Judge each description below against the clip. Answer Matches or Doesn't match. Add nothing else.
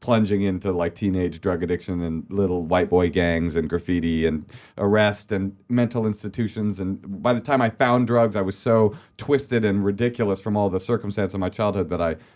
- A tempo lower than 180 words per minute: Doesn't match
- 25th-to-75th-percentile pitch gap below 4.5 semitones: Matches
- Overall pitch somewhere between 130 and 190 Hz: Doesn't match